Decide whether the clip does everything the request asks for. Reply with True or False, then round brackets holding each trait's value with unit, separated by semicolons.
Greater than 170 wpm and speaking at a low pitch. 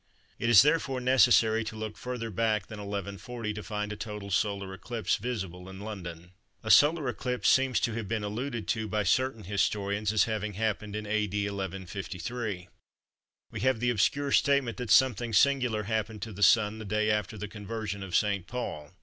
True (180 wpm; 105 Hz)